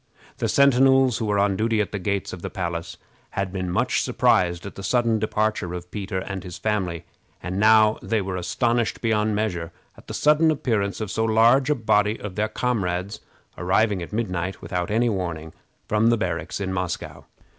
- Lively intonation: No, average, 3.5 semitones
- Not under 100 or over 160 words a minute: No, average, 190 wpm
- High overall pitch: No, low, 105 Hz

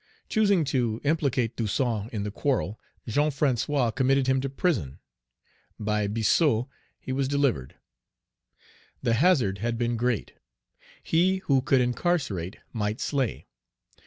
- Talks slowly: Yes, slow, 125 wpm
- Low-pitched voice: Yes, low, 125 Hz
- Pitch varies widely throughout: No, average, 4.3 semitones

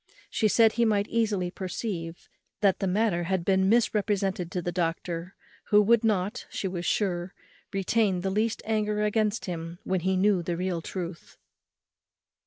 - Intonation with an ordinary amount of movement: Yes, average, 3.1 semitones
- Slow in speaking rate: No, average, 160 wpm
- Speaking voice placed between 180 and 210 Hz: Yes, high, 190 Hz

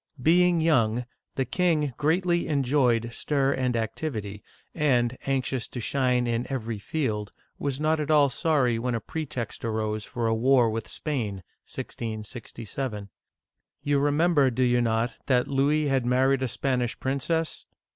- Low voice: Yes, low, 130 Hz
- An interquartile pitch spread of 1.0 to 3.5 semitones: No, average, 4.0 semitones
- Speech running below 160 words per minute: Yes, average, 145 wpm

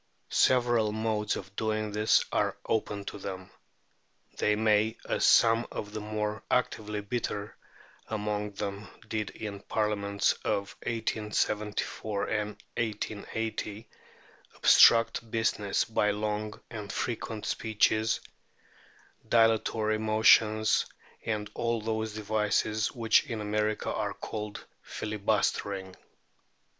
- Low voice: Yes, low, 110 Hz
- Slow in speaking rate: Yes, slow, 105 wpm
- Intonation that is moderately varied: No, narrow, 1.0 semitones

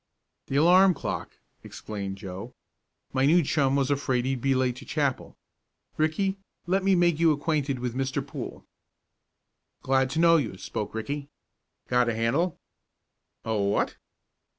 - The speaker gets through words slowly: No, average, 145 wpm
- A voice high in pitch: No, low, 135 Hz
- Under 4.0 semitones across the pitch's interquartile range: No, average, 4.7 semitones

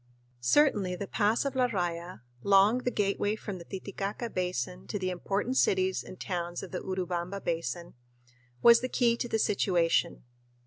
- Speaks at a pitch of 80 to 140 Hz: No, high, 190 Hz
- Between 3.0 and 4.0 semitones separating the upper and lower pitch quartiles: Yes, average, 3.5 semitones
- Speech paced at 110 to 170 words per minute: Yes, average, 165 wpm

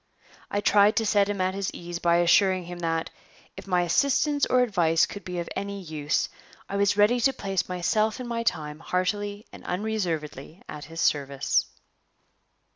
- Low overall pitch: No, medium, 185 Hz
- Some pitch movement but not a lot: Yes, average, 3.5 semitones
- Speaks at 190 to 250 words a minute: No, average, 175 wpm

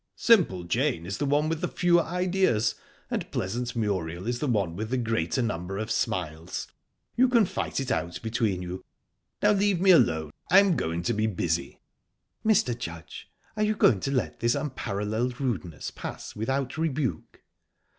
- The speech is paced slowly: No, average, 165 wpm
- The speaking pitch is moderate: No, low, 120 Hz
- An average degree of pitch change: No, wide, 9.0 semitones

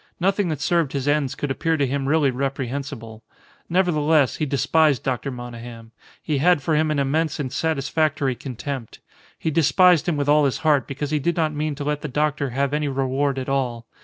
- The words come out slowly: No, average, 195 wpm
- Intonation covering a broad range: No, narrow, 2.6 semitones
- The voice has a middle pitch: Yes, medium, 145 Hz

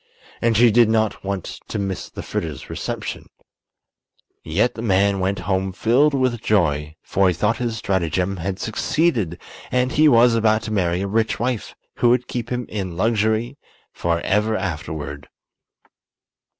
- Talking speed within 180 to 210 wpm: No, average, 150 wpm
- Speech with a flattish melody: No, average, 4.0 semitones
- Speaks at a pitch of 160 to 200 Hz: No, low, 105 Hz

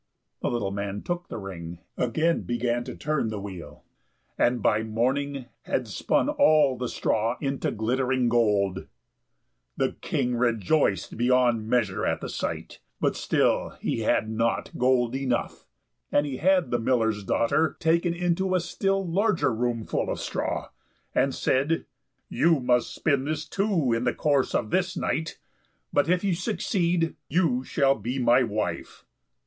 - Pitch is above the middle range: No, low, 125 Hz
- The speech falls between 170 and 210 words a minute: No, average, 155 wpm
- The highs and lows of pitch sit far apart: Yes, wide, 5.9 semitones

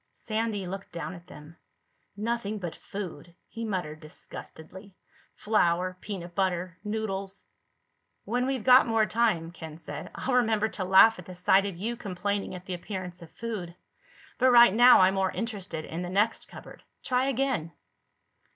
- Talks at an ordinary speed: Yes, average, 160 wpm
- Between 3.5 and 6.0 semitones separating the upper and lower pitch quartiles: Yes, average, 4.0 semitones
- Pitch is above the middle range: Yes, high, 195 Hz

